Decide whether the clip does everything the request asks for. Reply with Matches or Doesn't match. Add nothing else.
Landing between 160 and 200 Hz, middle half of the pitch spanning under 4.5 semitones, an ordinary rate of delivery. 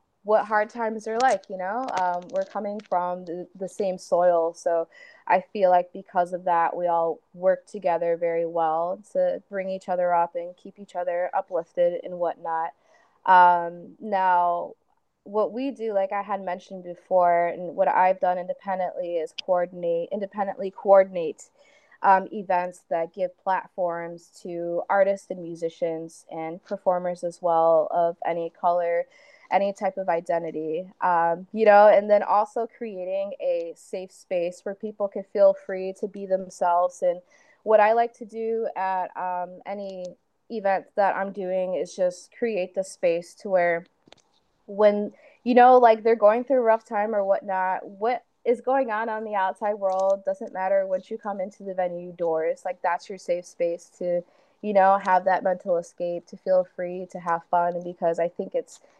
Matches